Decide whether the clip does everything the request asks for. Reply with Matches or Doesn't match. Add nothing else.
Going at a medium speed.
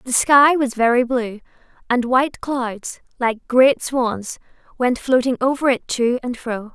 Matches